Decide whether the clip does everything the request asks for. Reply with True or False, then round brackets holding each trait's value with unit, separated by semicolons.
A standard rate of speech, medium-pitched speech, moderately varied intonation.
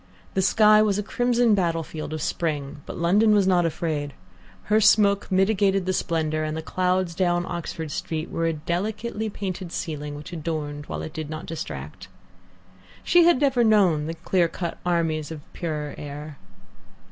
True (170 wpm; 170 Hz; 4.3 semitones)